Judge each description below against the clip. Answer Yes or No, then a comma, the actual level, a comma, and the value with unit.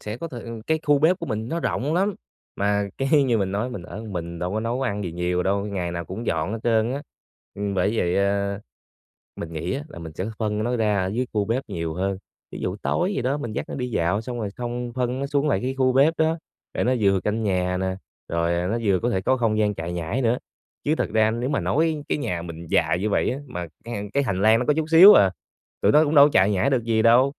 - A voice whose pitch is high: No, low, 110 Hz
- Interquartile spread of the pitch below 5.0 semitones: No, average, 5.3 semitones